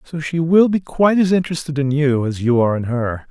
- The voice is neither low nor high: Yes, medium, 150 Hz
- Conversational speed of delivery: No, fast, 255 wpm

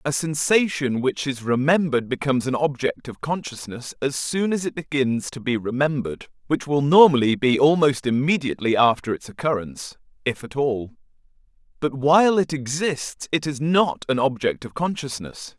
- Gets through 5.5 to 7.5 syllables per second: No, 5.1 syllables/s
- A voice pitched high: No, medium, 140 Hz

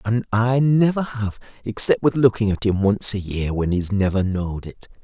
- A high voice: No, low, 105 Hz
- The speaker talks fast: Yes, fast, 215 wpm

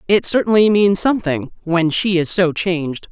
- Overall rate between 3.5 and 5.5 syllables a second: Yes, 5.0 syllables/s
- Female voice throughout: Yes, female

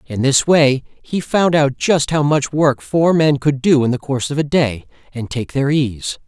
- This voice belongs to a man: Yes, male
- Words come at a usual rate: No, fast, 220 wpm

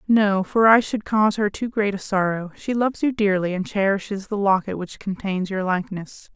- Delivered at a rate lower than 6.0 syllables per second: Yes, 5.2 syllables/s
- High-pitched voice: Yes, high, 200 Hz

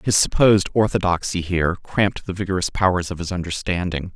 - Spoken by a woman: No, male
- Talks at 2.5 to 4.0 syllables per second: No, 5.9 syllables/s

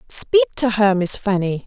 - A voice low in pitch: No, high, 220 Hz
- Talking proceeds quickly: No, average, 180 wpm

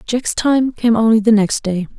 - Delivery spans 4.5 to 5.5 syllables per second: Yes, 4.6 syllables/s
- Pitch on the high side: Yes, high, 225 Hz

